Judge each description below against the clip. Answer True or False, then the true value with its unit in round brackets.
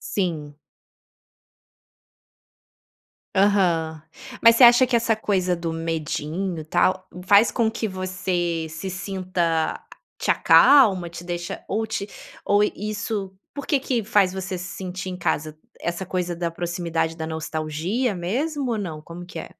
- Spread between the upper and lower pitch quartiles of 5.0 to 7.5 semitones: False (3.6 semitones)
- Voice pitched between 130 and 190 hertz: True (185 Hz)